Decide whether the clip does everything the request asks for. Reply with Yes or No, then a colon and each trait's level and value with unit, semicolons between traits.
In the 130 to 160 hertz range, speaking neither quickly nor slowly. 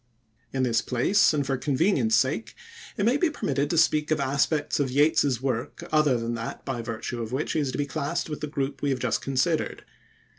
No: medium, 140 Hz; fast, 215 wpm